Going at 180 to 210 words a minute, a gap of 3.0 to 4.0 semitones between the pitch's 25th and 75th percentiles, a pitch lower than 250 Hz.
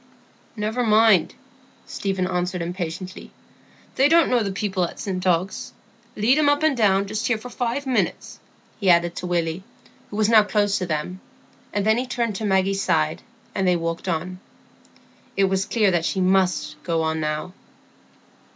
No: average, 170 wpm; average, 3.6 semitones; high, 190 Hz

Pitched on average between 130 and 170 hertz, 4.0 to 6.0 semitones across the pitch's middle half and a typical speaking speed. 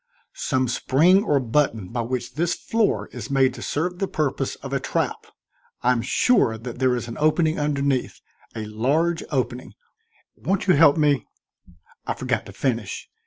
Yes: low, 135 Hz; average, 4.4 semitones; average, 165 wpm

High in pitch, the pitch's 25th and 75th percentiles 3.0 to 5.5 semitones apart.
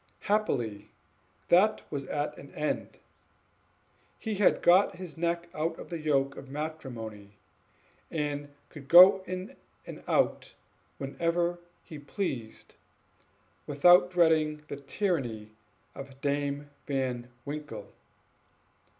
No: medium, 150 Hz; average, 4.0 semitones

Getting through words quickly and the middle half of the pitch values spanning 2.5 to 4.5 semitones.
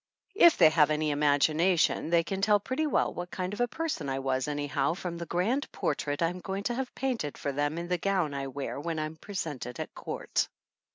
No: fast, 215 wpm; average, 5.2 semitones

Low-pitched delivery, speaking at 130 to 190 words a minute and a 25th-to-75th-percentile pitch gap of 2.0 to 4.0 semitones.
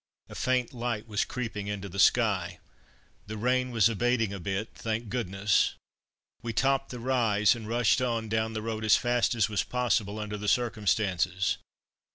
Yes: low, 110 Hz; average, 170 wpm; average, 2.8 semitones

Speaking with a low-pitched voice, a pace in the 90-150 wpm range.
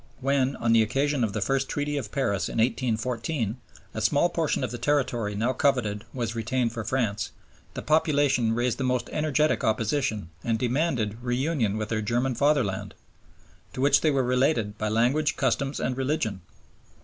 No: low, 125 Hz; average, 170 wpm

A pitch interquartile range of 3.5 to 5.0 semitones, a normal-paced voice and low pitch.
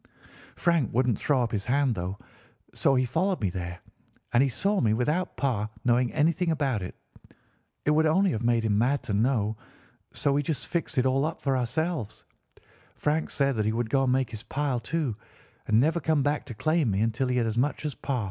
No: average, 4.7 semitones; fast, 215 wpm; low, 130 Hz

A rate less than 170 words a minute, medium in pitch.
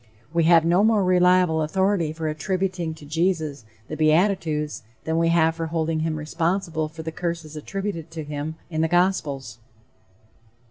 Yes: average, 155 wpm; medium, 165 Hz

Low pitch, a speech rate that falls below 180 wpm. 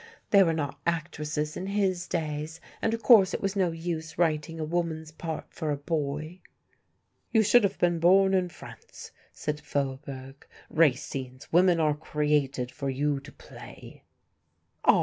No: medium, 160 Hz; average, 155 wpm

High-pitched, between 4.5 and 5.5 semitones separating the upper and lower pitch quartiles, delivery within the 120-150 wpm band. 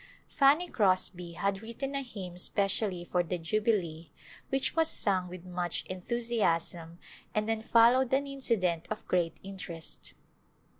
Yes: high, 195 Hz; average, 4.9 semitones; slow, 135 wpm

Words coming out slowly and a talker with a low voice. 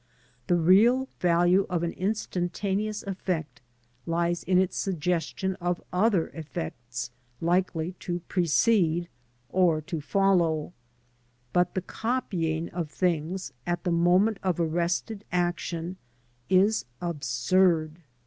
No: slow, 110 wpm; medium, 175 Hz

